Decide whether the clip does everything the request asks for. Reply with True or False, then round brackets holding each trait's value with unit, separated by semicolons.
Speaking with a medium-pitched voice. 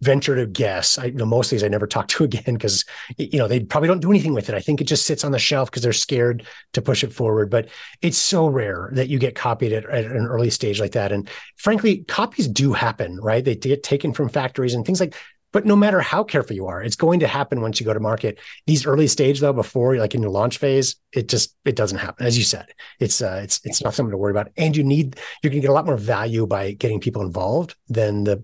False (125 Hz)